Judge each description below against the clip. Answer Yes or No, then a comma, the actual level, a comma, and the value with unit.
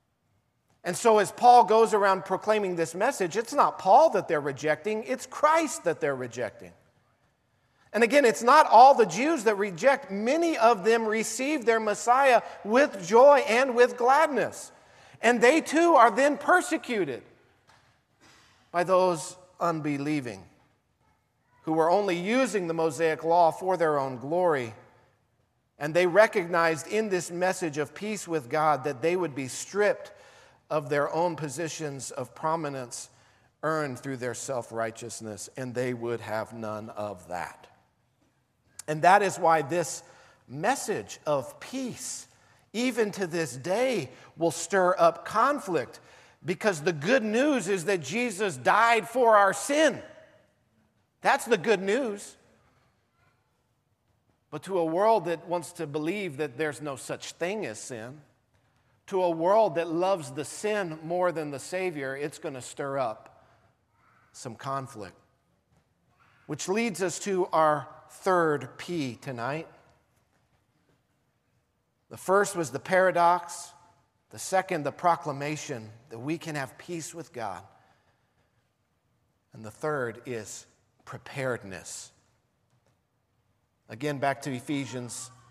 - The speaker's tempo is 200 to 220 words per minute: No, slow, 135 wpm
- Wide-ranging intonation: Yes, wide, 7.4 semitones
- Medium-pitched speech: Yes, medium, 165 Hz